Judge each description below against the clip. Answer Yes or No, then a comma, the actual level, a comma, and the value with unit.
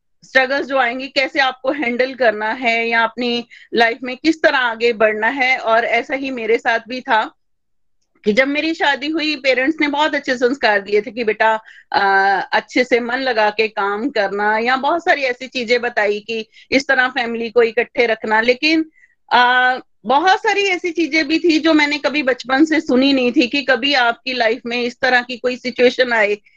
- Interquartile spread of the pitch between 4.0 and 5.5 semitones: No, average, 3.4 semitones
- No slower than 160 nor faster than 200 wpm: Yes, fast, 190 wpm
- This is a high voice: Yes, very high, 250 Hz